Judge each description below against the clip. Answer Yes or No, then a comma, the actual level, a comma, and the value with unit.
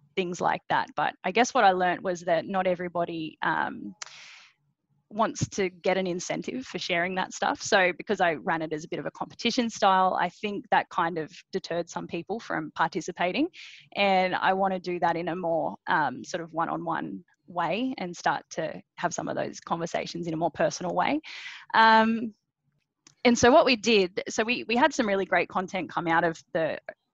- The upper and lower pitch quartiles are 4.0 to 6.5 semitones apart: Yes, average, 4.6 semitones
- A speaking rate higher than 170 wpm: Yes, fast, 205 wpm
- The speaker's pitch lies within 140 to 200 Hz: Yes, medium, 185 Hz